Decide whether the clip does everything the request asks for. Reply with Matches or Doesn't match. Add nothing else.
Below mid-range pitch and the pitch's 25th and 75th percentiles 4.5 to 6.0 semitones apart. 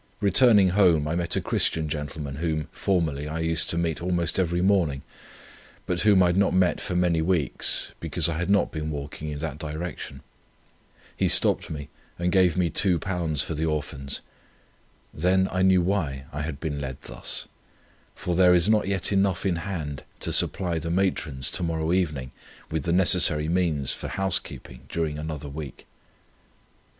Doesn't match